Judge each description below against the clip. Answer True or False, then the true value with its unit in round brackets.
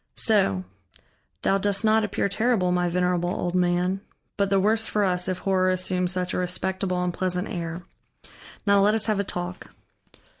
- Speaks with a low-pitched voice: False (185 Hz)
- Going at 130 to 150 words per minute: False (175 wpm)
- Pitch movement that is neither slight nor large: False (2.0 semitones)